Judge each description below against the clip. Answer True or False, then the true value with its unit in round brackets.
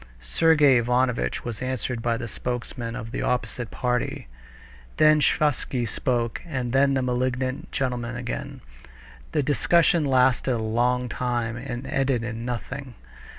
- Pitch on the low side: True (125 Hz)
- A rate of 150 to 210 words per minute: False (135 wpm)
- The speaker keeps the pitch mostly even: True (1.9 semitones)